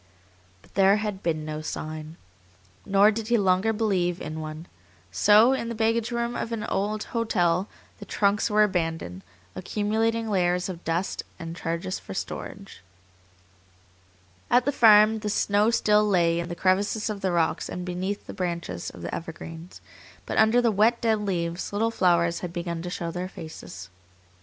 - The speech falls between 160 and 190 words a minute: Yes, average, 165 wpm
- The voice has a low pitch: No, high, 190 Hz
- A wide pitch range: No, average, 4.1 semitones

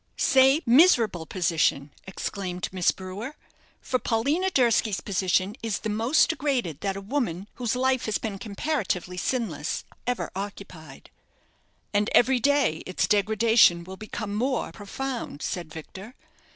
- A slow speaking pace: Yes, slow, 130 wpm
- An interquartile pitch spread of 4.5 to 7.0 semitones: Yes, average, 5.3 semitones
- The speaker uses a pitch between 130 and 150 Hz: No, high, 210 Hz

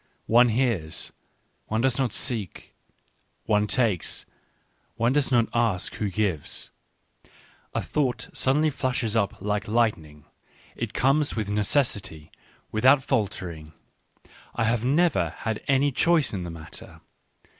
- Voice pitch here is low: Yes, low, 115 Hz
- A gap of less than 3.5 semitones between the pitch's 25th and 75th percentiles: No, average, 4.8 semitones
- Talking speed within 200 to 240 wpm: No, slow, 135 wpm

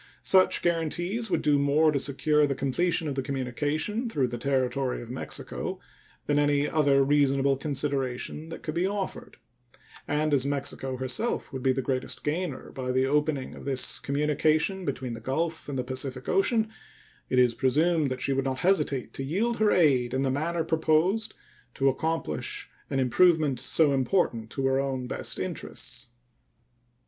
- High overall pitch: No, medium, 140 Hz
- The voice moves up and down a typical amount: Yes, average, 3.4 semitones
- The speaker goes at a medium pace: Yes, average, 165 wpm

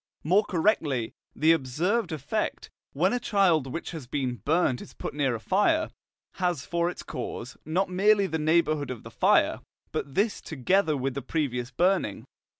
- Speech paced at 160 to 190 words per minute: Yes, average, 165 wpm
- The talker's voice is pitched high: No, medium, 160 Hz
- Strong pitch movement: Yes, wide, 5.7 semitones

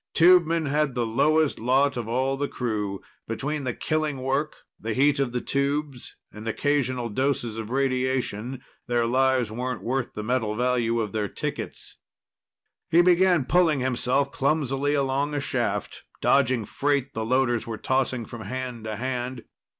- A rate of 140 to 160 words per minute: Yes, average, 155 wpm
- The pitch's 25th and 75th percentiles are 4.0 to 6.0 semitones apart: No, average, 3.1 semitones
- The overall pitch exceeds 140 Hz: No, low, 130 Hz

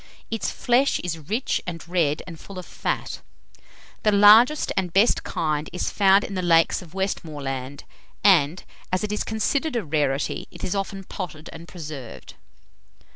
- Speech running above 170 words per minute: No, average, 160 wpm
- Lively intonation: No, average, 4.7 semitones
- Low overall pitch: No, medium, 180 Hz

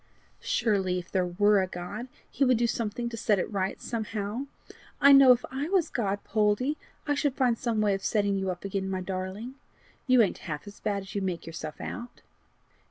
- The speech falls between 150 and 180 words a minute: No, fast, 205 wpm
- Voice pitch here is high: Yes, high, 210 Hz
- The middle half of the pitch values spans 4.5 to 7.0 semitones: No, average, 4.1 semitones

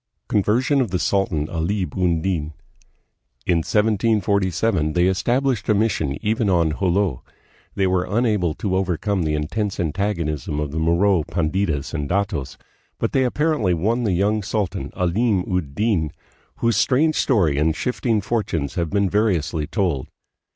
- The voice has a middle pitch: No, very low, 95 Hz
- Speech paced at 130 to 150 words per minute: Yes, average, 145 wpm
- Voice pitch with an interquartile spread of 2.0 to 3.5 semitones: No, average, 4.6 semitones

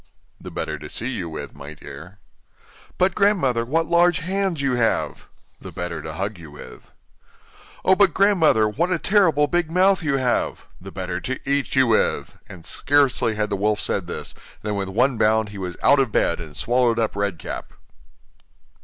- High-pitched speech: No, low, 125 Hz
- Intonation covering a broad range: Yes, wide, 8.5 semitones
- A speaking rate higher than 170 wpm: Yes, average, 185 wpm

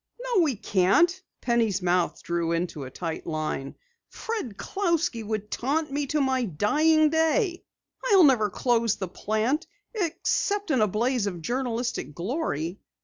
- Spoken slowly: No, average, 145 wpm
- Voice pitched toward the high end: Yes, high, 240 Hz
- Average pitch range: No, wide, 8.9 semitones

